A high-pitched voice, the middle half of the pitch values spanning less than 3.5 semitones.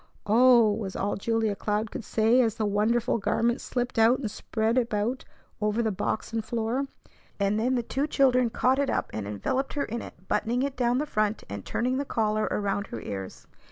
Yes: high, 225 Hz; average, 3.1 semitones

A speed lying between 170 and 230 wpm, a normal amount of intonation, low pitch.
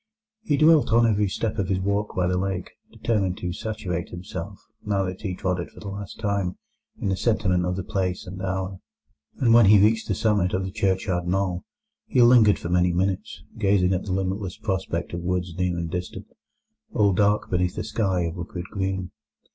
No: average, 200 wpm; narrow, 2.3 semitones; very low, 95 Hz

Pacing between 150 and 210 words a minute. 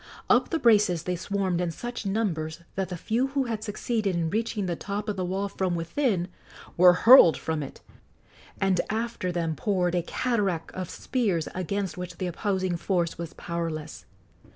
Yes: average, 175 wpm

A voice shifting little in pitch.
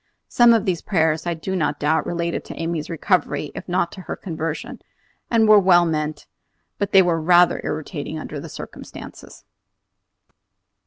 No: average, 3.0 semitones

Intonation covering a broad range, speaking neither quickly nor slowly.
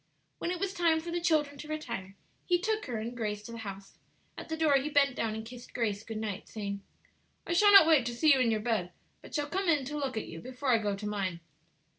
No: wide, 6.6 semitones; fast, 260 wpm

